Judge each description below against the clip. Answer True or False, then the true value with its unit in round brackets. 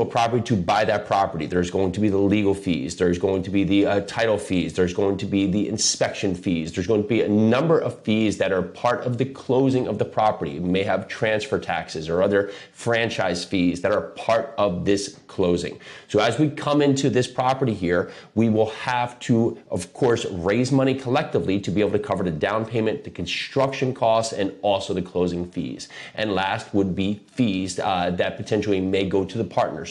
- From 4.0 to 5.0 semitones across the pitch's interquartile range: False (3.4 semitones)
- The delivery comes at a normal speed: False (210 wpm)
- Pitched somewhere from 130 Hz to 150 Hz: False (105 Hz)